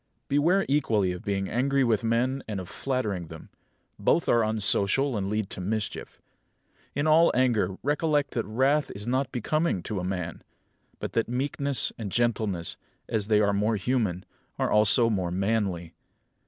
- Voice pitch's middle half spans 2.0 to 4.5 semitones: No, average, 5.2 semitones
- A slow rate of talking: No, average, 160 wpm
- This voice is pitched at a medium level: No, low, 110 Hz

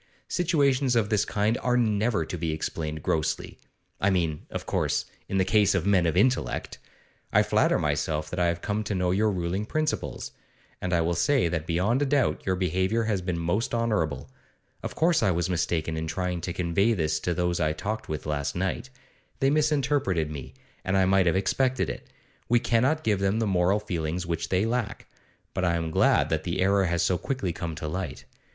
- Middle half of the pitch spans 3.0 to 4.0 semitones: No, average, 4.7 semitones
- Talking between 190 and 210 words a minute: Yes, average, 200 wpm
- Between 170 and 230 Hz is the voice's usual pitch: No, very low, 95 Hz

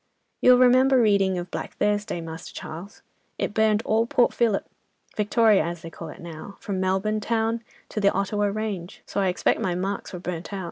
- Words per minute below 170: No, average, 190 wpm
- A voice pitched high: Yes, high, 200 Hz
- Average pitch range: Yes, average, 3.4 semitones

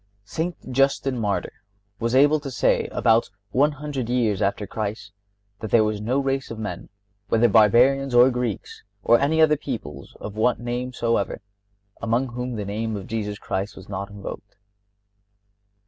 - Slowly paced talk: No, average, 160 wpm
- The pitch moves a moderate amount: Yes, average, 4.2 semitones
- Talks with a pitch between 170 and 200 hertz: No, low, 115 Hz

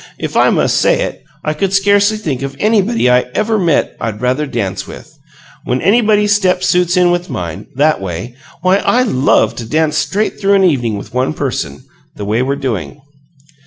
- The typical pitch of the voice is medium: Yes, medium, 155 Hz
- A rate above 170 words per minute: Yes, average, 190 wpm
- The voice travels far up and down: Yes, wide, 8.2 semitones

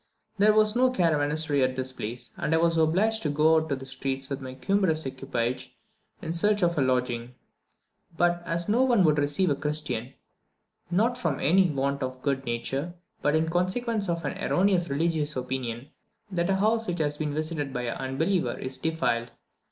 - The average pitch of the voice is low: No, medium, 155 Hz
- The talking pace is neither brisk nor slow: Yes, average, 185 wpm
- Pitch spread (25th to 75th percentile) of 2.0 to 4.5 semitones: No, average, 4.9 semitones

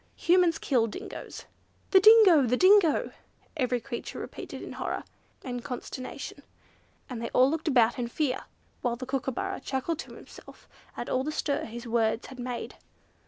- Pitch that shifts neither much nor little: Yes, average, 4.7 semitones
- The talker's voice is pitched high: Yes, very high, 260 Hz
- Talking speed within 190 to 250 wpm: No, average, 160 wpm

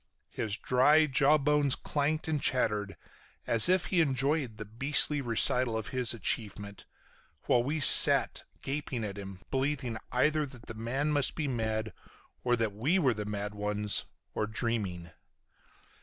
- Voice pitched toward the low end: Yes, low, 125 Hz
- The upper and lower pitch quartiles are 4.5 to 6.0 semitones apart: Yes, average, 5.1 semitones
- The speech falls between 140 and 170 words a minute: Yes, average, 150 wpm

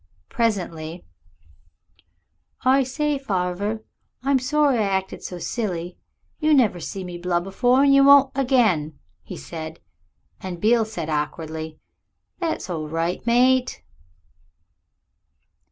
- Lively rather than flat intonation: Yes, wide, 7.2 semitones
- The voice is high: Yes, high, 200 Hz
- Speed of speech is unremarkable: No, slow, 115 wpm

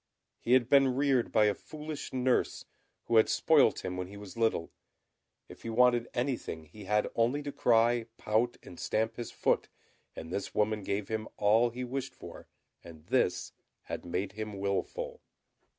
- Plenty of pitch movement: No, average, 3.8 semitones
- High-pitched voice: No, low, 115 Hz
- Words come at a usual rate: Yes, average, 170 wpm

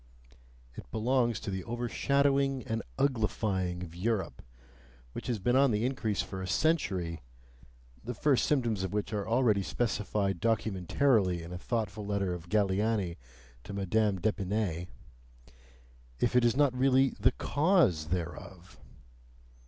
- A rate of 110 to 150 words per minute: Yes, slow, 135 wpm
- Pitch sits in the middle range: No, low, 105 Hz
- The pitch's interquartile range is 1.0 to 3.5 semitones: No, average, 4.7 semitones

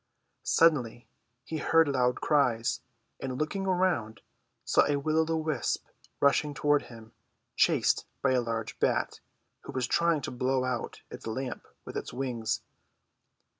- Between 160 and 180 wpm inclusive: No, average, 145 wpm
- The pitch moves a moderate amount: Yes, average, 4.2 semitones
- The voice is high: No, low, 135 Hz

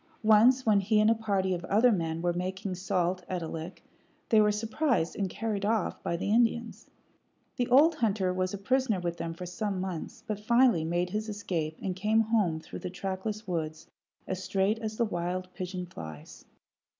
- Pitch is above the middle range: Yes, high, 195 Hz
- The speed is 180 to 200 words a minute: Yes, average, 190 wpm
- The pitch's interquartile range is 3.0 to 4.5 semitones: Yes, average, 3.6 semitones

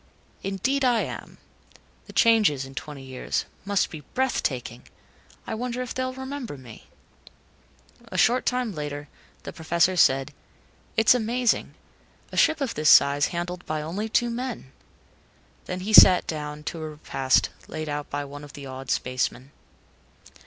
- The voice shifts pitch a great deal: Yes, wide, 8.2 semitones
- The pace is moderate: Yes, average, 150 wpm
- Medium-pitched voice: Yes, medium, 165 Hz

